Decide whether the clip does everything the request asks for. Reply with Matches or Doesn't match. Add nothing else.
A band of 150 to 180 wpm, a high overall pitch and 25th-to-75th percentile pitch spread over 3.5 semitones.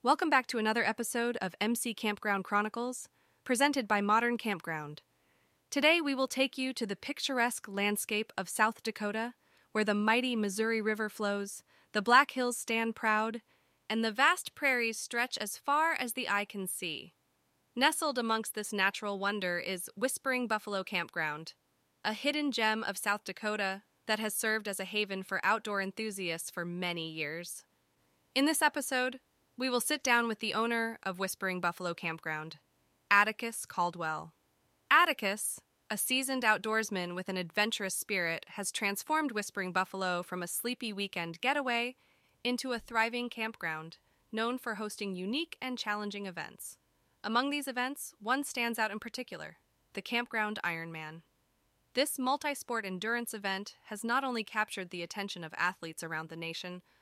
Matches